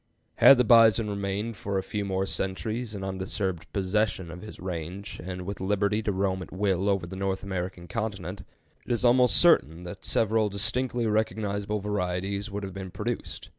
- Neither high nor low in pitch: No, low, 100 Hz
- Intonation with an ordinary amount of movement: No, narrow, 2.3 semitones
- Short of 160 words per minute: No, average, 175 wpm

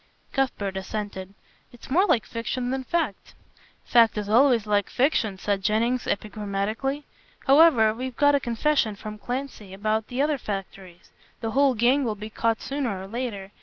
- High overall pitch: Yes, high, 225 Hz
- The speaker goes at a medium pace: Yes, average, 160 wpm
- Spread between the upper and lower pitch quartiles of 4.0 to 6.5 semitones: Yes, average, 4.3 semitones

